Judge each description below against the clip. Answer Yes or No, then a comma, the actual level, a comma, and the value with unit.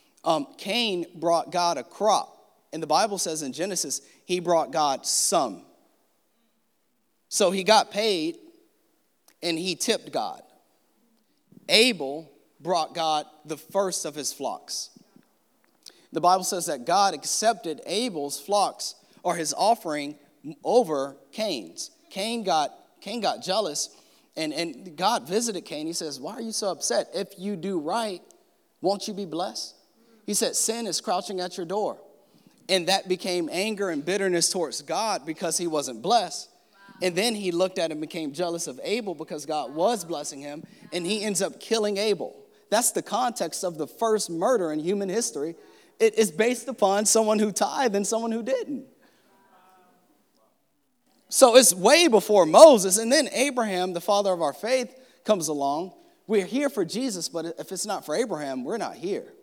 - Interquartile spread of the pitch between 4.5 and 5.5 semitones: Yes, average, 5.1 semitones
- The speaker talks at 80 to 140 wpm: No, average, 160 wpm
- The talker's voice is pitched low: No, high, 200 Hz